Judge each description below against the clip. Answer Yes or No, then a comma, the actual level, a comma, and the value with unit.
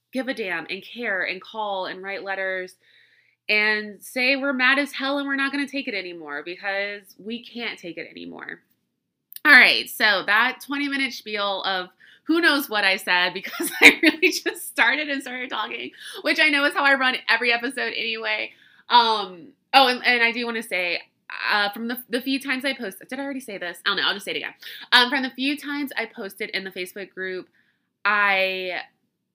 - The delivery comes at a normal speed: No, fast, 210 wpm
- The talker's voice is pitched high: Yes, high, 230 Hz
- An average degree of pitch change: No, wide, 5.9 semitones